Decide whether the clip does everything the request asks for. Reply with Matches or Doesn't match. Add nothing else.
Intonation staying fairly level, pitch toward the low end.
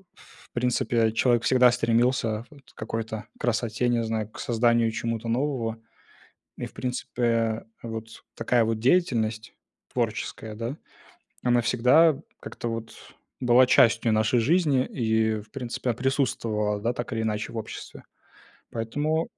Matches